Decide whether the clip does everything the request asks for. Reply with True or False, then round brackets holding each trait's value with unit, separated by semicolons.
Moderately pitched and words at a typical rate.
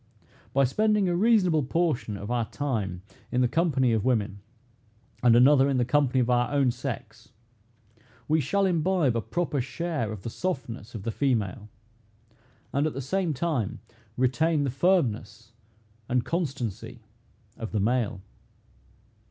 False (130 Hz; 145 wpm)